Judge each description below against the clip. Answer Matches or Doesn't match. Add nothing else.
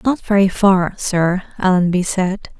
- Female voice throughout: Matches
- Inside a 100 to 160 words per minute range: Matches